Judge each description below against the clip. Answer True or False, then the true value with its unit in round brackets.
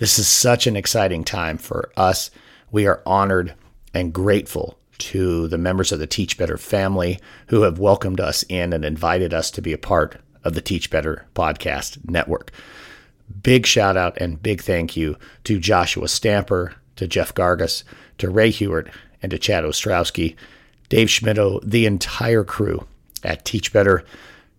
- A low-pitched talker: True (95 Hz)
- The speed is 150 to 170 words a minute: True (165 wpm)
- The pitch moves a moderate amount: True (3.5 semitones)